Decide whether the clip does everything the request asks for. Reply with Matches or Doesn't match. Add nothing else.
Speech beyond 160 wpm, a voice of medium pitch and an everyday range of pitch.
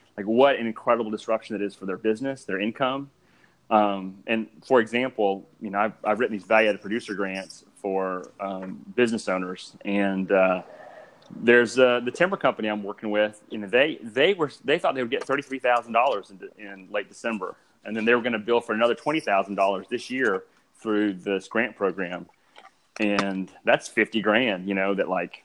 Doesn't match